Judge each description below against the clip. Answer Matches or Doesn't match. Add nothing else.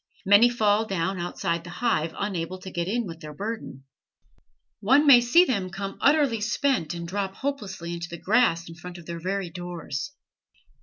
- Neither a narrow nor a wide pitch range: Matches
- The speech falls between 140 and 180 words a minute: Matches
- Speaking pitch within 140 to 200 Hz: Matches